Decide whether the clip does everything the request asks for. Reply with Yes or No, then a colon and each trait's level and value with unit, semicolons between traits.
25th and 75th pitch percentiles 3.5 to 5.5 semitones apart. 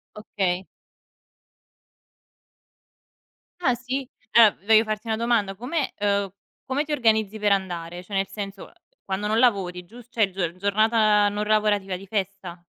No: narrow, 2.5 semitones